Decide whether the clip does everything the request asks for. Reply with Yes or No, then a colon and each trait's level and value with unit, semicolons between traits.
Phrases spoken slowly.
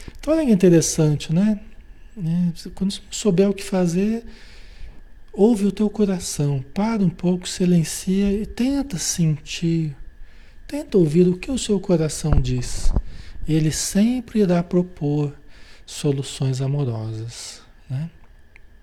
Yes: slow, 110 wpm